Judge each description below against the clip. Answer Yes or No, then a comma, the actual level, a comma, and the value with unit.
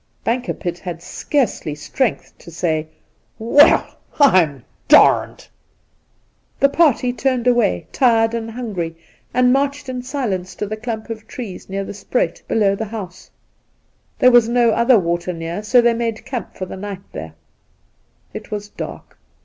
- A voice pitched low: No, high, 220 Hz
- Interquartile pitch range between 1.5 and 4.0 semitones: No, average, 5.0 semitones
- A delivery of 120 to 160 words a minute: Yes, average, 150 wpm